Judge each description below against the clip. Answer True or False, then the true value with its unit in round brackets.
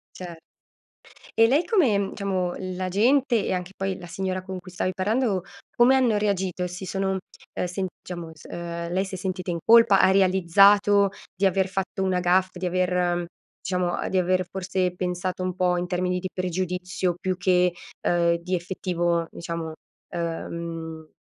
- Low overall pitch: False (185 Hz)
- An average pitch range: False (1.5 semitones)